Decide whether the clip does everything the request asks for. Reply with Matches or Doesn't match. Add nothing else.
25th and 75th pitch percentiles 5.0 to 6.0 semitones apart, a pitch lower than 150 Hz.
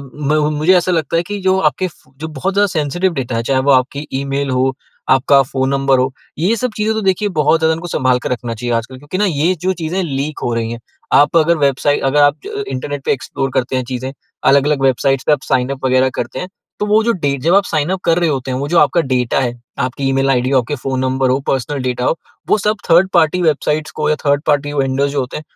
Doesn't match